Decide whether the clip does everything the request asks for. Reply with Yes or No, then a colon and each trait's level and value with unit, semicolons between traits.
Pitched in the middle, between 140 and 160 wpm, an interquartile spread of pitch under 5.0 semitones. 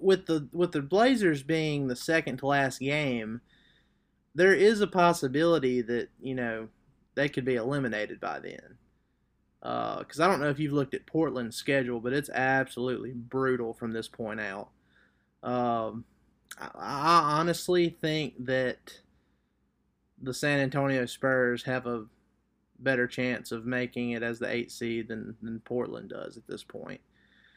No: low, 130 Hz; average, 155 wpm; average, 3.8 semitones